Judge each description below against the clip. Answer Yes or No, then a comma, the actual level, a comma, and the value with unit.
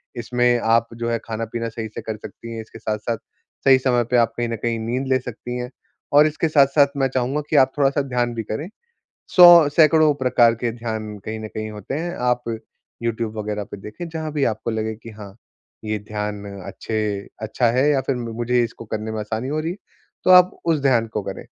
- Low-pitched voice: Yes, low, 120 Hz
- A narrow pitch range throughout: No, average, 3.4 semitones